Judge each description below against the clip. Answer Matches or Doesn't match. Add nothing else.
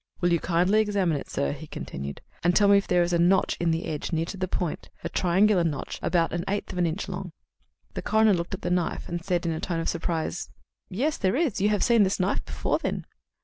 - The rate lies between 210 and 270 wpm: Matches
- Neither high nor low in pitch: Matches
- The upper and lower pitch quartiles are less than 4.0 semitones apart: Matches